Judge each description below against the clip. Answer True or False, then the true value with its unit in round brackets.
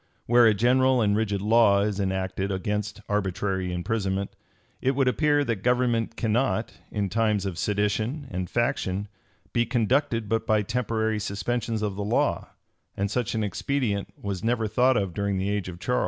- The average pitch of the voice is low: True (105 Hz)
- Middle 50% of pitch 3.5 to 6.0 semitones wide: False (3.0 semitones)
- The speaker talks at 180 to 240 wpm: False (170 wpm)